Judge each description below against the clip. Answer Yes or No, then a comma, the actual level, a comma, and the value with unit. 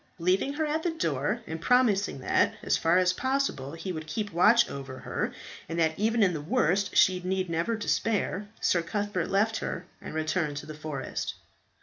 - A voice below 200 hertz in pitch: Yes, medium, 185 Hz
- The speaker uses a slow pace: No, average, 190 wpm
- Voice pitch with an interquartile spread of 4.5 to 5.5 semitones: Yes, average, 5.1 semitones